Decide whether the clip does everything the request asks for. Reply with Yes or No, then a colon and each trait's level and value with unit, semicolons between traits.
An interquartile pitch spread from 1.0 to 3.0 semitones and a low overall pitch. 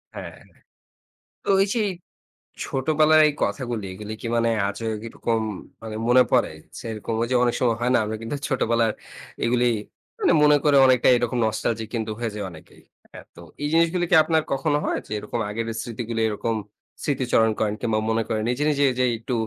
No: average, 3.5 semitones; low, 120 Hz